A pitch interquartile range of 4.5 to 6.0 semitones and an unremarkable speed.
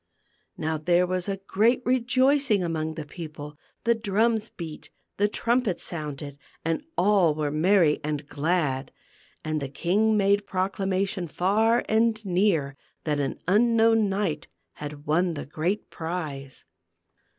No: wide, 5.6 semitones; slow, 130 wpm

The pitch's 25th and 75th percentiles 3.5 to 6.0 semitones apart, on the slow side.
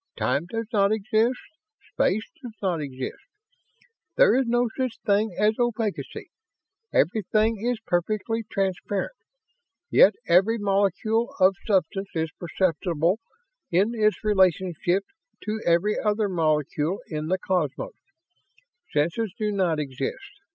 Yes: average, 4.1 semitones; slow, 115 wpm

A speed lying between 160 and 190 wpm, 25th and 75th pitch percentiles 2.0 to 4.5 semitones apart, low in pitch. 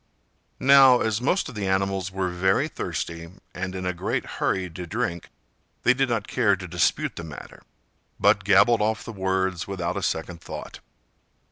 Yes: average, 175 wpm; average, 3.8 semitones; very low, 95 Hz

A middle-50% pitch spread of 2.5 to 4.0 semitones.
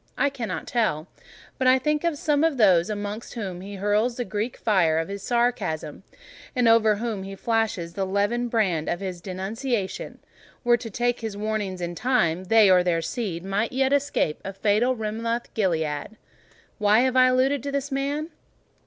No: average, 4.5 semitones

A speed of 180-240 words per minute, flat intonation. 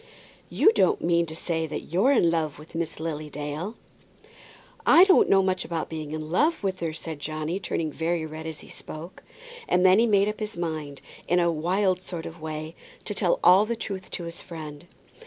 No: fast, 205 wpm; average, 3.3 semitones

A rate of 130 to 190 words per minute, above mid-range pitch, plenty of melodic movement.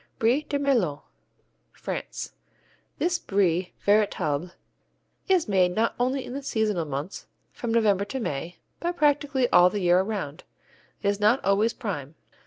Yes: average, 145 wpm; high, 210 Hz; wide, 6.4 semitones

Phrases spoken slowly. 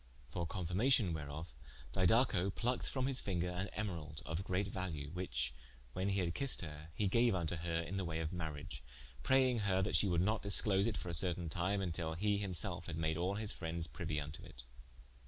No: fast, 205 wpm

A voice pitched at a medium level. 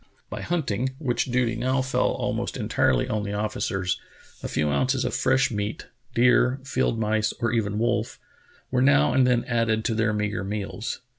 No: low, 115 Hz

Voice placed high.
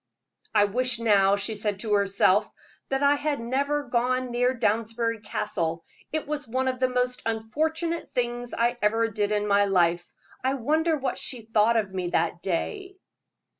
Yes: high, 230 Hz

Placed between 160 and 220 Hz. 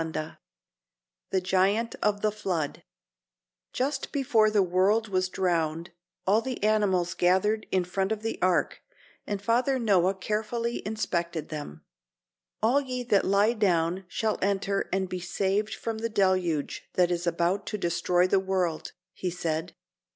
Yes: high, 190 Hz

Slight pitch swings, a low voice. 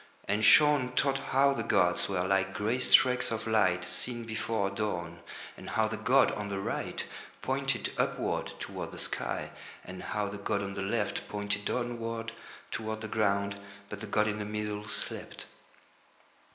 Yes: narrow, 2.3 semitones; low, 105 Hz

